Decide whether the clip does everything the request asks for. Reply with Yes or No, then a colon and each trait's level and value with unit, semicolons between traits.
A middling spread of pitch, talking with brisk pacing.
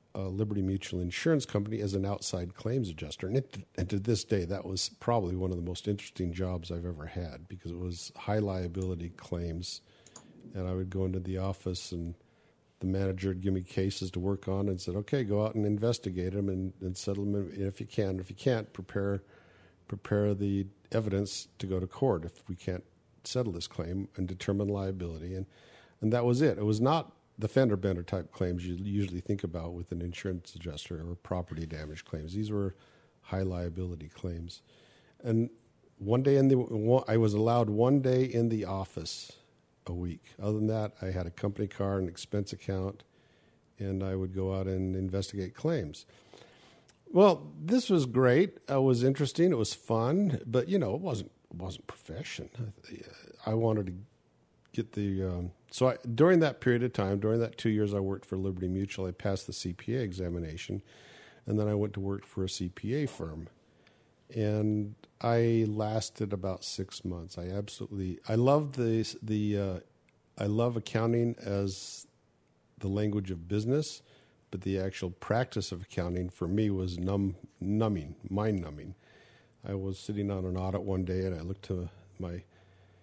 No: average, 3.3 semitones; average, 180 wpm